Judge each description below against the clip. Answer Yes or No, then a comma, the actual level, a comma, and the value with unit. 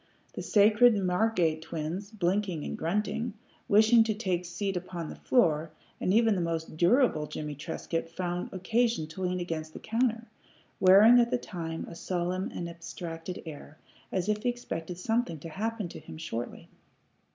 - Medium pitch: Yes, medium, 180 Hz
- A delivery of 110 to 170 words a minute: Yes, average, 165 wpm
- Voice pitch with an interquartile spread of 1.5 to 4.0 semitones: No, average, 4.7 semitones